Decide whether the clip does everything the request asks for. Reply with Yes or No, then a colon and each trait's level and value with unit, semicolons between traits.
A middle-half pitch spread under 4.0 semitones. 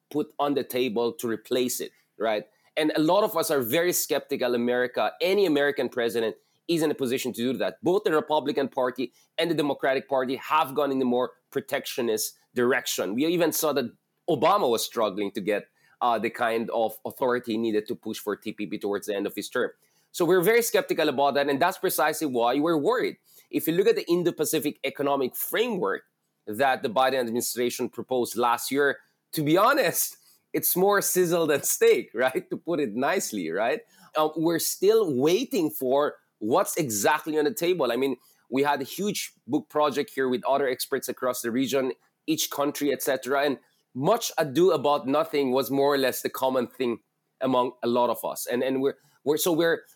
No: average, 4.6 semitones